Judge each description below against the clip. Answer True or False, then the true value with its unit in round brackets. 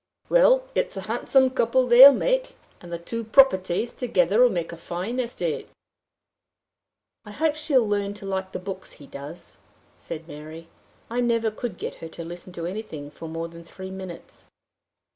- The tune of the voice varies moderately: False (6.2 semitones)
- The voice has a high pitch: True (195 Hz)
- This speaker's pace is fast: False (165 wpm)